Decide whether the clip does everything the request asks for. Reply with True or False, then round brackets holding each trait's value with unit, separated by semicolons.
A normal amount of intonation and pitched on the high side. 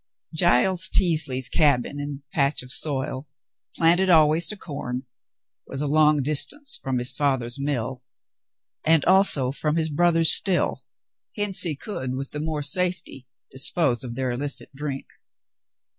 False (3.9 semitones; 145 Hz)